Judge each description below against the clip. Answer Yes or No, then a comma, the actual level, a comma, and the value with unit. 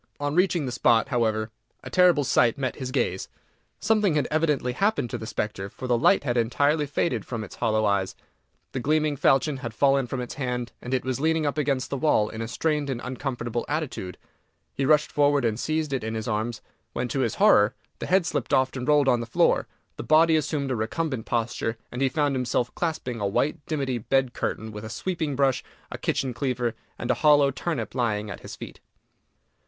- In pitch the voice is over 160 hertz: No, low, 130 Hz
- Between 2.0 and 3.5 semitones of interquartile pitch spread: No, average, 4.1 semitones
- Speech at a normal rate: No, fast, 210 wpm